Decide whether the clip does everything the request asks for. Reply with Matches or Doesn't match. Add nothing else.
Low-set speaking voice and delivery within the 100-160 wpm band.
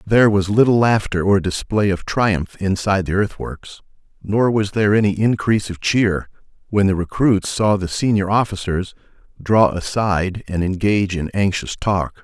Matches